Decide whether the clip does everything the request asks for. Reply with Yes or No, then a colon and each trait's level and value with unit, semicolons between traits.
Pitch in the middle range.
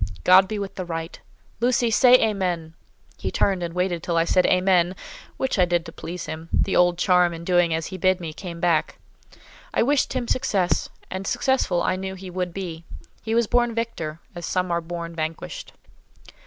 Yes: medium, 180 Hz